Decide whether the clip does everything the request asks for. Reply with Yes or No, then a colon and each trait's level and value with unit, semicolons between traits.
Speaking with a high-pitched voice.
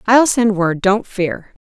Yes: high, 205 Hz